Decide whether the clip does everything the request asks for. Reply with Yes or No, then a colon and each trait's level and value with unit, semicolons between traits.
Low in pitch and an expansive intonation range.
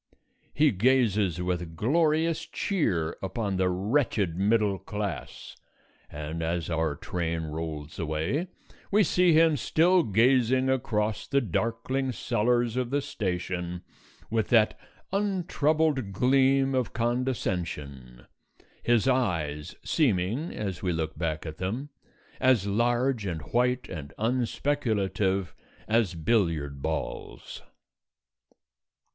Yes: low, 110 Hz; wide, 7.1 semitones